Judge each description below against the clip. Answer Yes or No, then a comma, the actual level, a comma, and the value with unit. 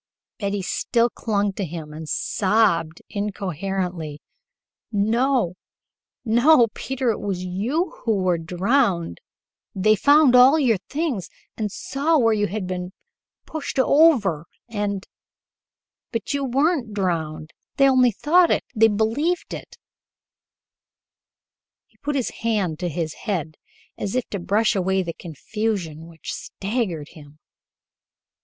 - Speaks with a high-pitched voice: Yes, high, 205 Hz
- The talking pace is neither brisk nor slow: No, slow, 125 wpm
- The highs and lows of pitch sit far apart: Yes, wide, 5.8 semitones